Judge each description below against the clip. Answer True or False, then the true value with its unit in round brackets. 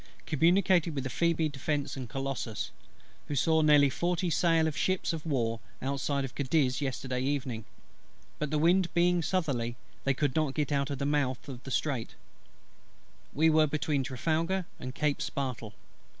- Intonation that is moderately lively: True (3.3 semitones)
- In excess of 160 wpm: False (155 wpm)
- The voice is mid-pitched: True (145 Hz)